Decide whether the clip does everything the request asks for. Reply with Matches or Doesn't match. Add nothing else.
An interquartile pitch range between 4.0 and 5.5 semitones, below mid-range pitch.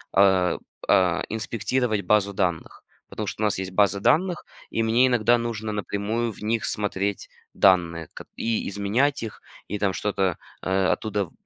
Doesn't match